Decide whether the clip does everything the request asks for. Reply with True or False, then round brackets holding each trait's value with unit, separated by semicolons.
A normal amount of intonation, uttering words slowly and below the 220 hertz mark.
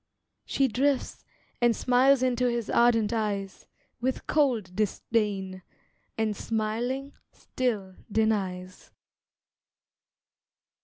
False (3.5 semitones; 85 wpm; 225 Hz)